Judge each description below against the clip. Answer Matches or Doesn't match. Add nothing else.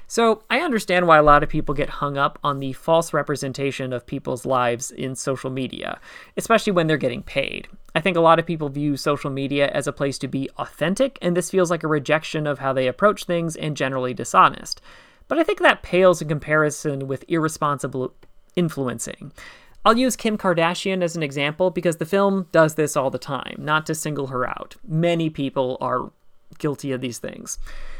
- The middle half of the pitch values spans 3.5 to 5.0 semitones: Matches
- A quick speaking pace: Doesn't match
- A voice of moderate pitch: Matches